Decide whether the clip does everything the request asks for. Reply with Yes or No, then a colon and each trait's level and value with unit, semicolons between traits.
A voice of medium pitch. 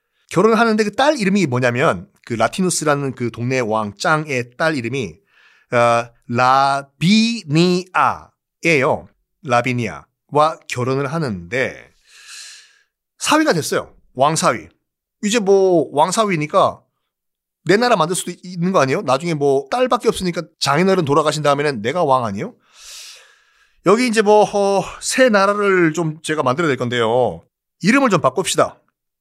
Yes: medium, 170 Hz